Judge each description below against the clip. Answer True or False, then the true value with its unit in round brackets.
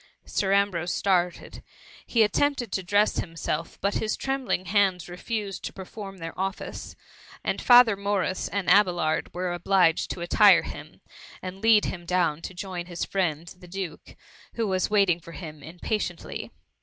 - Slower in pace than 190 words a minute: True (155 wpm)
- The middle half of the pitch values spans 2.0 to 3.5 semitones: True (2.7 semitones)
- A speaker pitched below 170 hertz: False (185 Hz)